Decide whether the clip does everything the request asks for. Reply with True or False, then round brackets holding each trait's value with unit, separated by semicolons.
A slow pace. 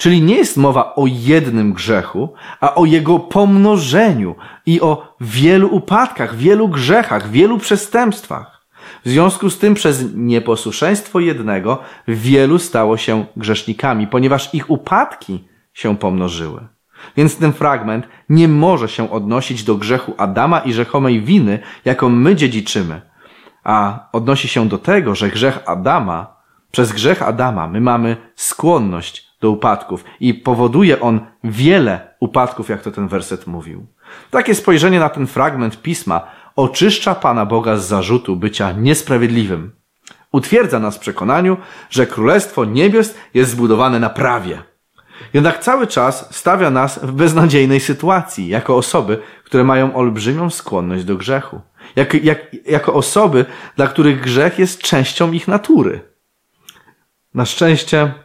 False (135 wpm)